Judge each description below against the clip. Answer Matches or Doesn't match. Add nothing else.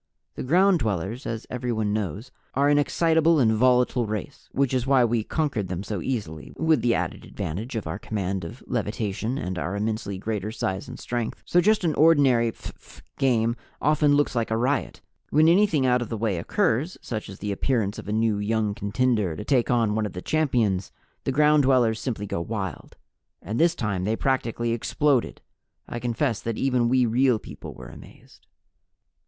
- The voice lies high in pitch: Doesn't match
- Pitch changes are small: Doesn't match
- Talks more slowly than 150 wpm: Doesn't match